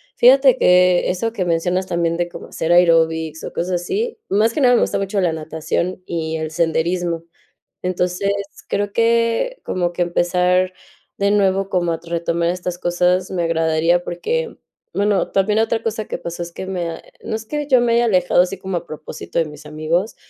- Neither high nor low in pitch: Yes, medium, 180 Hz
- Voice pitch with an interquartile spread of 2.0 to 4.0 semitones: Yes, average, 3.2 semitones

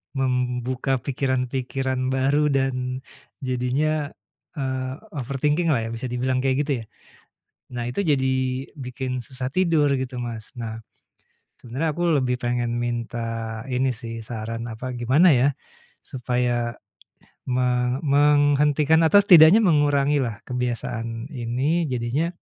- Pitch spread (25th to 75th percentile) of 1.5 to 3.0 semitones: Yes, average, 2.7 semitones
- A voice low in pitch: Yes, low, 130 Hz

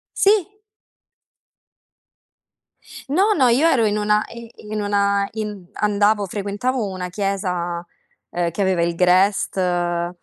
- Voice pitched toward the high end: Yes, high, 200 Hz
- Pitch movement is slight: No, average, 3.1 semitones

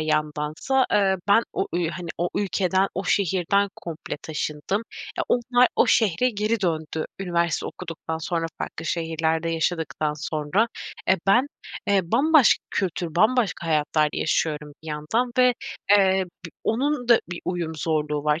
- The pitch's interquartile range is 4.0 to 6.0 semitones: Yes, average, 4.6 semitones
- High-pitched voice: No, medium, 175 Hz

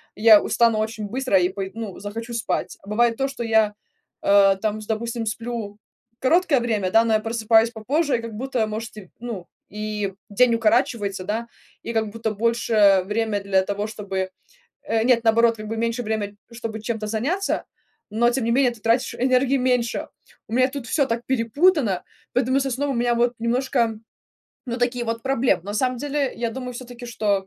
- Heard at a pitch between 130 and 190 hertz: No, high, 230 Hz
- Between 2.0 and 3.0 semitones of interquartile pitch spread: Yes, narrow, 2.5 semitones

